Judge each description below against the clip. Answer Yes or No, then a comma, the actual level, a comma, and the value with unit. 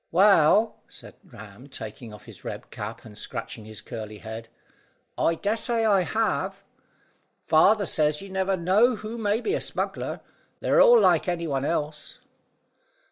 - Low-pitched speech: No, medium, 175 Hz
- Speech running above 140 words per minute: Yes, average, 150 wpm